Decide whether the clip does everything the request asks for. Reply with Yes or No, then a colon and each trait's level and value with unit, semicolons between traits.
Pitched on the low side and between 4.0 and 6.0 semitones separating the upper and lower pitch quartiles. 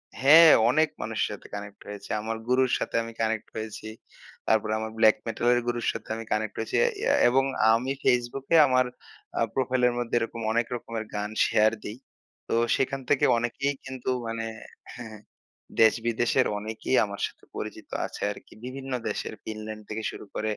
No: low, 115 Hz; average, 2.7 semitones